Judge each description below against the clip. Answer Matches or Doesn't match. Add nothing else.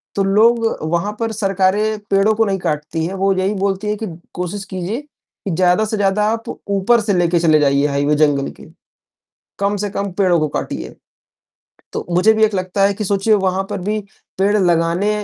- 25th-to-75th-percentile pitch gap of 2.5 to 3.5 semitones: Matches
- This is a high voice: Matches